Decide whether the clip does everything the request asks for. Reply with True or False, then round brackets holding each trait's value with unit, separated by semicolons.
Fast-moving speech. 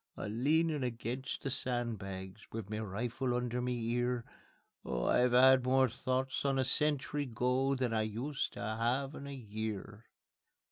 False (160 wpm)